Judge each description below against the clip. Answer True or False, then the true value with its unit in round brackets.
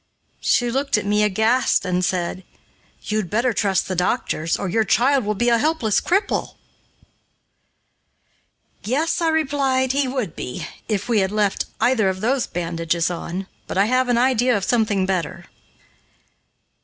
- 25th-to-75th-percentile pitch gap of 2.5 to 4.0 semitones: False (5.2 semitones)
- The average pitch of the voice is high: True (220 Hz)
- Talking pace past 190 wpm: False (155 wpm)